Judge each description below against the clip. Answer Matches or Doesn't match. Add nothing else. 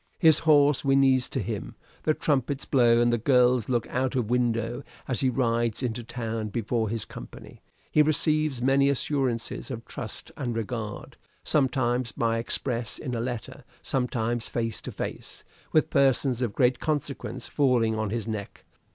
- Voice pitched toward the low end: Matches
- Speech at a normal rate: Matches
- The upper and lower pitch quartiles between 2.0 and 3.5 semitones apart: Matches